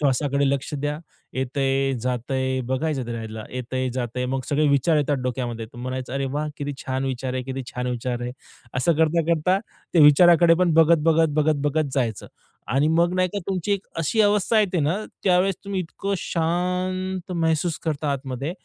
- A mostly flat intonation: No, average, 4.6 semitones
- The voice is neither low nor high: Yes, medium, 145 Hz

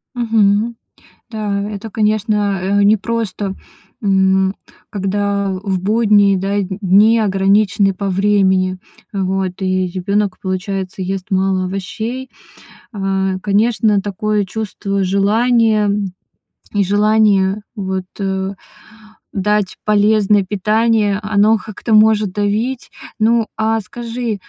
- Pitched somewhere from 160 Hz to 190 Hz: No, high, 205 Hz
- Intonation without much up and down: Yes, narrow, 2.0 semitones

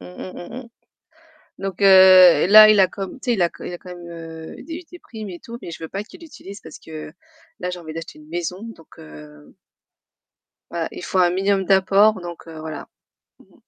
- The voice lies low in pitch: No, medium, 180 Hz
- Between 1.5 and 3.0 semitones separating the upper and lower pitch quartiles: No, average, 3.6 semitones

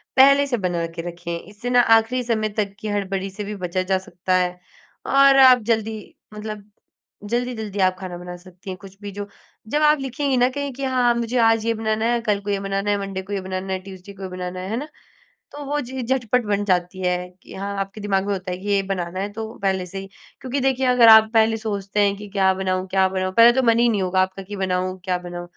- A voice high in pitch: Yes, high, 200 Hz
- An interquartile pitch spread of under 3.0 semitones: No, average, 3.6 semitones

